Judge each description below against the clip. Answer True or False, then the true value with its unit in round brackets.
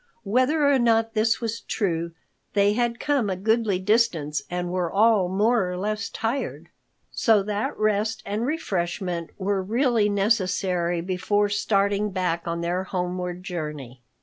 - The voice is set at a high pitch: True (200 Hz)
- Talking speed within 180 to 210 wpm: False (145 wpm)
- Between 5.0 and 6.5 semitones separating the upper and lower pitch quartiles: False (3.7 semitones)